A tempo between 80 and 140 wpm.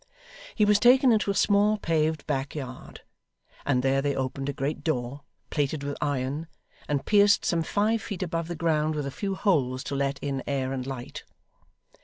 No: average, 185 wpm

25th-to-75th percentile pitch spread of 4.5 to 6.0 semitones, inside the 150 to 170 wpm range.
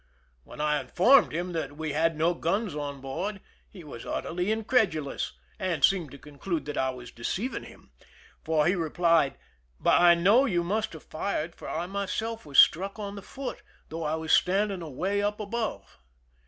No: average, 4.8 semitones; average, 180 wpm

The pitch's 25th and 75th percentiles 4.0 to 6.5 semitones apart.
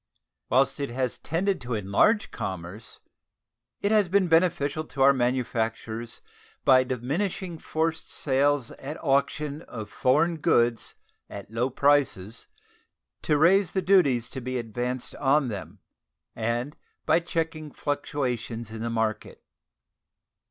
Yes: average, 5.1 semitones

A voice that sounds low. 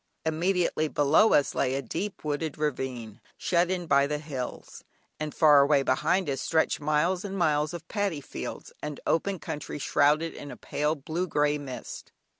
No: medium, 150 Hz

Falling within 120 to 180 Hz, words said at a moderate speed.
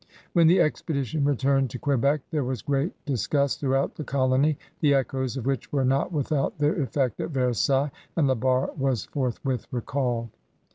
Yes: low, 135 Hz; average, 175 wpm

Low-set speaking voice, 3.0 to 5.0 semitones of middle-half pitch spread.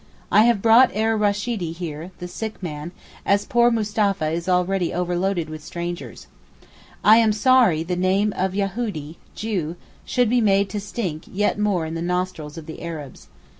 No: high, 190 Hz; average, 4.0 semitones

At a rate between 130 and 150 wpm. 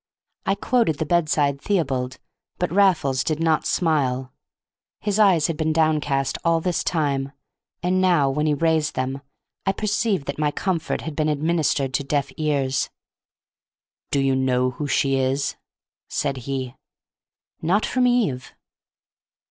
Yes: average, 140 wpm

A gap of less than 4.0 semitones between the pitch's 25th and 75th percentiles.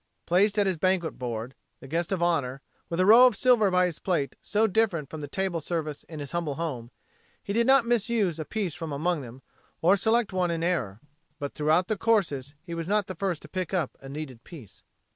No: average, 4.8 semitones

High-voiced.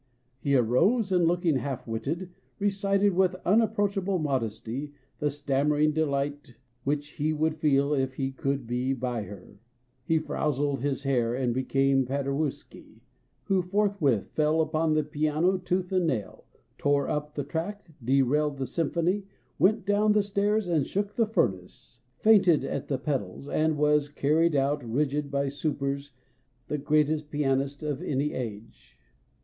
No: medium, 150 Hz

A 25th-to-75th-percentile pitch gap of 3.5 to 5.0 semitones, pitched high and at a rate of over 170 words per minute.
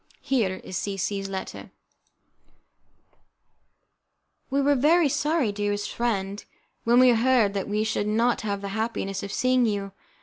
No: average, 4.1 semitones; high, 215 Hz; average, 145 wpm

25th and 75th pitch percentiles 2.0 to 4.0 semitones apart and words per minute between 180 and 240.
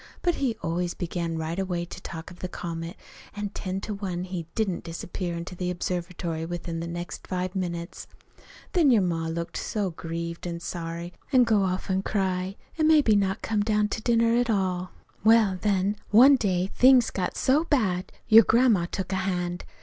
Yes: average, 3.6 semitones; average, 190 wpm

